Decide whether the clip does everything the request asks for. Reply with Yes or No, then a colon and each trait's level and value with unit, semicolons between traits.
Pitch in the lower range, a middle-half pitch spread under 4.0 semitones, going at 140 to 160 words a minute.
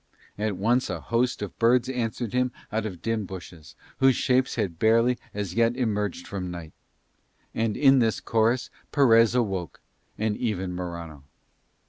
No: low, 110 Hz; average, 4.4 semitones; average, 150 wpm